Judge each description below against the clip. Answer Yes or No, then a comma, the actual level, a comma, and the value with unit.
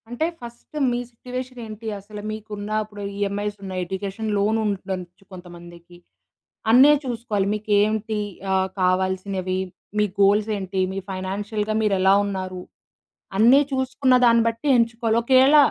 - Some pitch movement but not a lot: Yes, average, 3.3 semitones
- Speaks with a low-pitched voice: No, high, 210 Hz